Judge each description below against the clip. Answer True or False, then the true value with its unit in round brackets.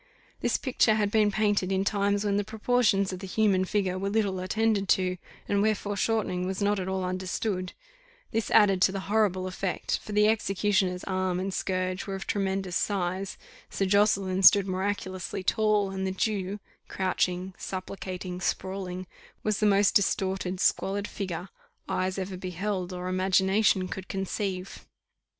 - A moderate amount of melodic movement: False (1.7 semitones)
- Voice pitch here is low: False (195 Hz)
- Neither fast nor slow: True (155 wpm)